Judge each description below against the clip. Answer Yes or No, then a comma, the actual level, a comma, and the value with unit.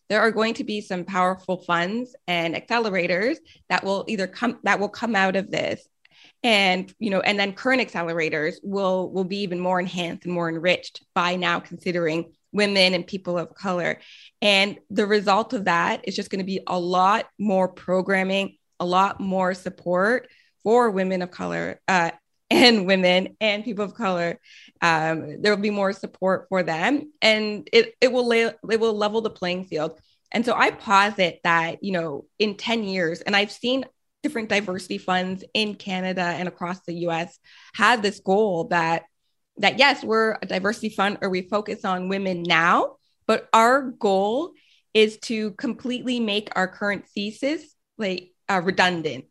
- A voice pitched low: No, high, 195 Hz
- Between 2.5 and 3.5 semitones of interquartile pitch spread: Yes, average, 3.2 semitones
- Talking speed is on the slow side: No, average, 175 wpm